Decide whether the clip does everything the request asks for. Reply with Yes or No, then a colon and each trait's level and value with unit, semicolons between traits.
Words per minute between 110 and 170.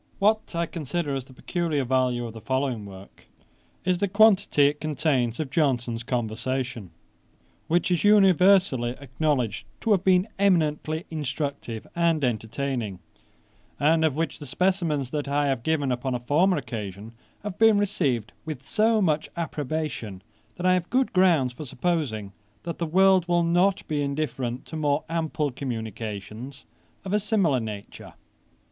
Yes: average, 150 wpm